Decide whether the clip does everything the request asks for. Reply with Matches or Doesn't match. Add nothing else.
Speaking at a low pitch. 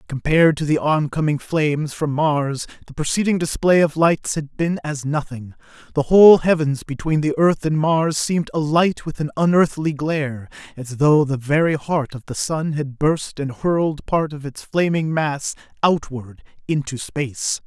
Doesn't match